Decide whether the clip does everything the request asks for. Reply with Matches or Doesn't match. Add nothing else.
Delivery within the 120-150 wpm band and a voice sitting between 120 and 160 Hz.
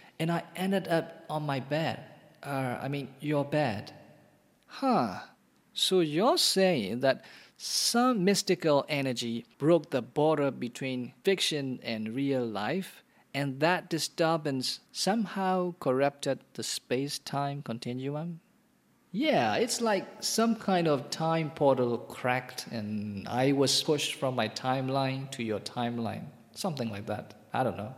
Matches